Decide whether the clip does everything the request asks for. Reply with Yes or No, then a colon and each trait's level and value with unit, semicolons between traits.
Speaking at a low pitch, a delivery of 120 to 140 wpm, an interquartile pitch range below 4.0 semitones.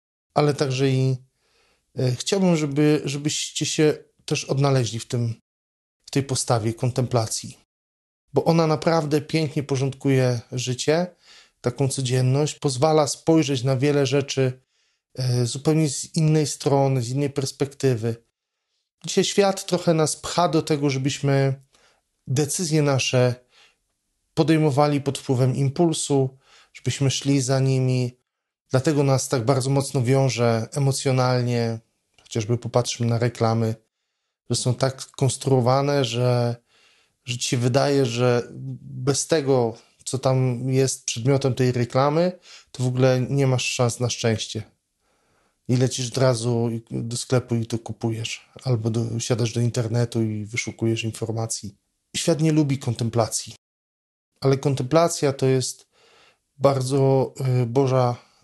Yes: low, 130 Hz; average, 125 wpm; average, 2.8 semitones